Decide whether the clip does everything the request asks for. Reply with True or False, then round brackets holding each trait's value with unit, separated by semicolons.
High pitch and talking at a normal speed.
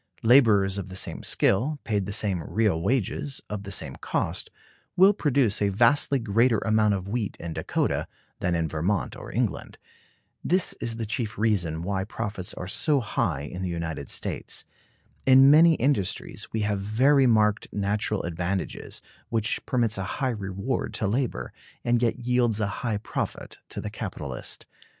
False (105 Hz; 165 wpm)